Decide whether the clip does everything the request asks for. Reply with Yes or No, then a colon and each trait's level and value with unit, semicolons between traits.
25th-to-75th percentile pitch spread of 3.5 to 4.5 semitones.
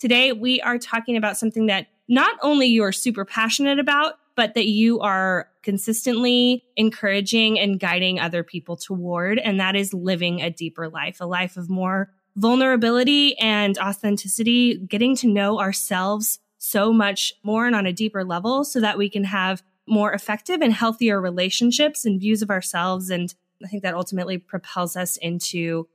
Yes: average, 3.8 semitones